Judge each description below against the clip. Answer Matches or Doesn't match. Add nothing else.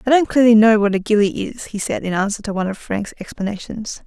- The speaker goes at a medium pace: Doesn't match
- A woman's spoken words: Matches